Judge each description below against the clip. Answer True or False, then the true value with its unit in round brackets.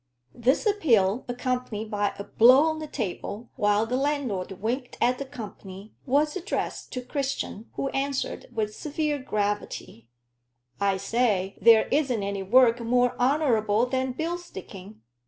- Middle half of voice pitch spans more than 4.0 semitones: True (4.8 semitones)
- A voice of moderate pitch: False (245 Hz)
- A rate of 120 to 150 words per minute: True (140 wpm)